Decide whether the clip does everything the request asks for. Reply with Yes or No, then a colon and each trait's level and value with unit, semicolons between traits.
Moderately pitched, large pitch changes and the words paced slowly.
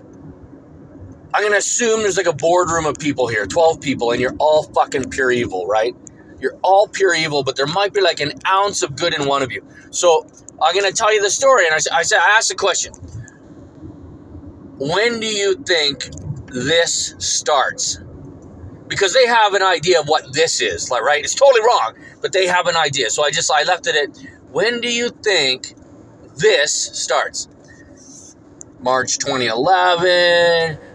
No: medium, 175 Hz; wide, 6.1 semitones; average, 180 wpm